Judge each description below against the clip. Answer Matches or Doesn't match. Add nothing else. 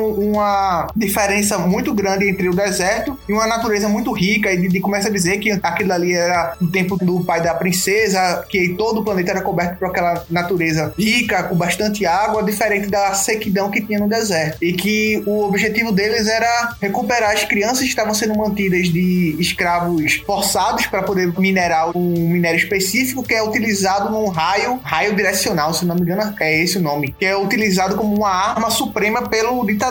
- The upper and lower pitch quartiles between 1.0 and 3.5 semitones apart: Matches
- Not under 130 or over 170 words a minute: Doesn't match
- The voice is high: Matches